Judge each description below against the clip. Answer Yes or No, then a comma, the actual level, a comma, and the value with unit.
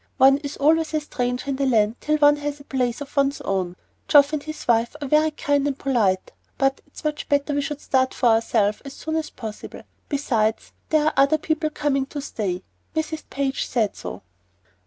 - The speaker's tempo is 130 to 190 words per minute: No, average, 200 wpm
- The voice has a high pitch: Yes, very high, 280 Hz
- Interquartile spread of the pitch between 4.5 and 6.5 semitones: No, average, 3.4 semitones